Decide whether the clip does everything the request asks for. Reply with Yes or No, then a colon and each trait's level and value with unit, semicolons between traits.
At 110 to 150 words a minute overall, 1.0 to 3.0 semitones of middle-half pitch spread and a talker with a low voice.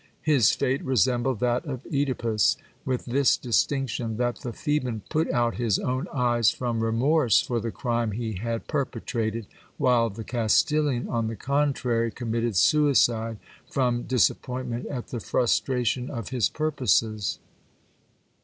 Yes: average, 140 wpm; narrow, 2.5 semitones; low, 120 Hz